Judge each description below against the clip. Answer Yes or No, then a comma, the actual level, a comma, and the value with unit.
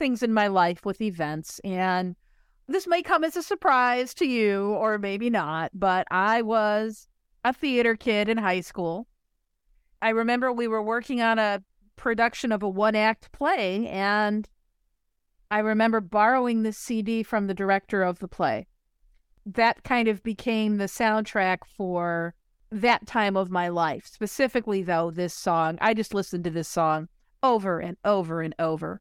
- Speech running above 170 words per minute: No, average, 165 wpm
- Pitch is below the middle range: No, high, 210 Hz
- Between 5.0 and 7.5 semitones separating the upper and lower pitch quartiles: No, average, 3.7 semitones